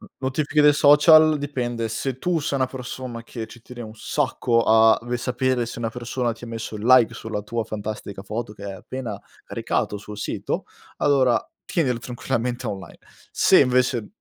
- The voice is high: No, low, 120 Hz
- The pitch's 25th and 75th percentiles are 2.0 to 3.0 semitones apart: Yes, average, 2.7 semitones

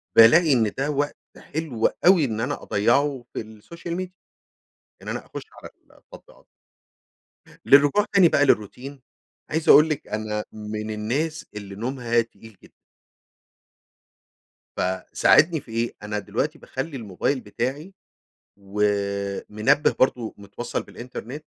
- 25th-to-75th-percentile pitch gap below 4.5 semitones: No, wide, 5.5 semitones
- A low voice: Yes, low, 120 Hz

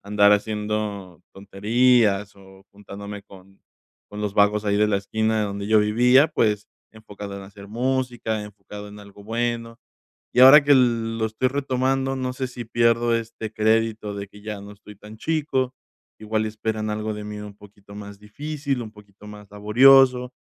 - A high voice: No, low, 105 Hz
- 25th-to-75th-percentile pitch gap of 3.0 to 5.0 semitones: No, narrow, 2.6 semitones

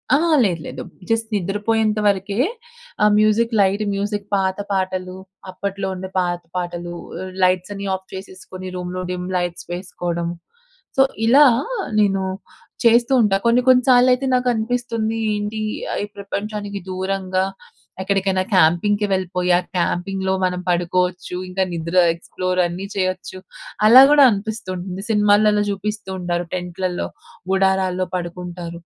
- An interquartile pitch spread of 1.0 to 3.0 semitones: Yes, narrow, 2.5 semitones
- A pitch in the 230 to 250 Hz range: No, high, 190 Hz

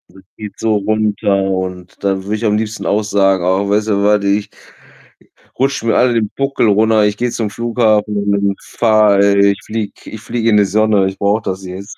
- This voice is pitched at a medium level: No, low, 105 Hz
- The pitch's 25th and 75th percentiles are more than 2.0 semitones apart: No, narrow, 1.7 semitones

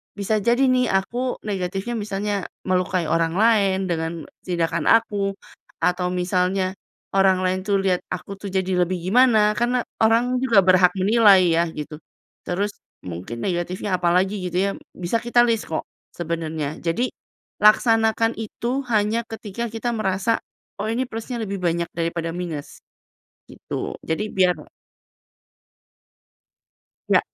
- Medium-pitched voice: No, high, 195 Hz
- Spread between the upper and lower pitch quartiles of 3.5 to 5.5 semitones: Yes, average, 3.9 semitones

